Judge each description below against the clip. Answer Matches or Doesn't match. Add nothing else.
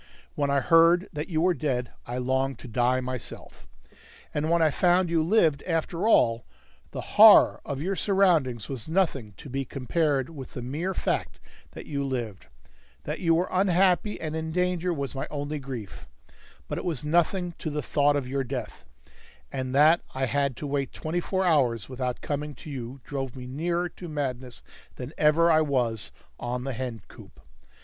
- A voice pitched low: Doesn't match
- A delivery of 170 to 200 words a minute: Matches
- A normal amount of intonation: Matches